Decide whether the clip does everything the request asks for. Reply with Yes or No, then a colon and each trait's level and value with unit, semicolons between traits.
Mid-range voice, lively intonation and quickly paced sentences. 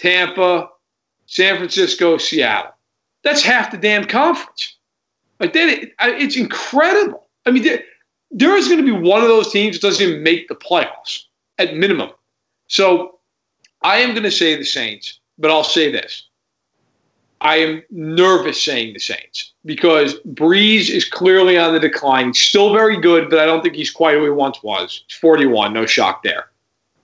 No: medium, 180 Hz; wide, 5.9 semitones; average, 175 wpm